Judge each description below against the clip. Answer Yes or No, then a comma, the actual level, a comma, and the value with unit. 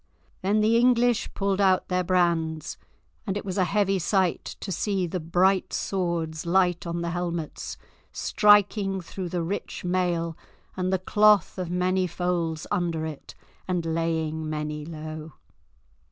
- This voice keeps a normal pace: Yes, average, 145 wpm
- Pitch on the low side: No, medium, 180 Hz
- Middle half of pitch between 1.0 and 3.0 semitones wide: Yes, average, 2.7 semitones